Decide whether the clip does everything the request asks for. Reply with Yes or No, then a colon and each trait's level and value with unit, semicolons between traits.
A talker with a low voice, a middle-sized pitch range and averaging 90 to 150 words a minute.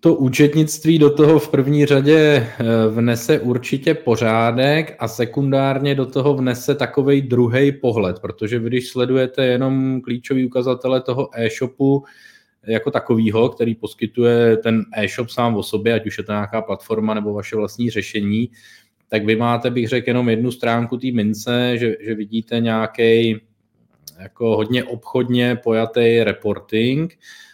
Yes: low, 120 Hz; average, 3.0 semitones; average, 140 wpm